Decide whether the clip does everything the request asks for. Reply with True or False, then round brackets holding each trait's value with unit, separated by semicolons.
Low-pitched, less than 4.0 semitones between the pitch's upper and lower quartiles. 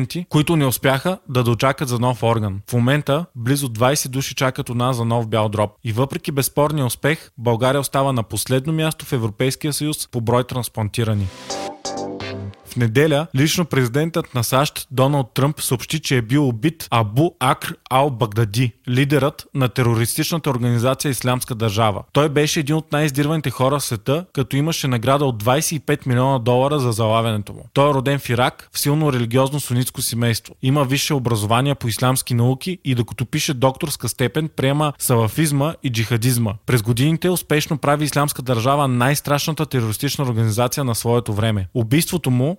True (130 Hz; 3.3 semitones)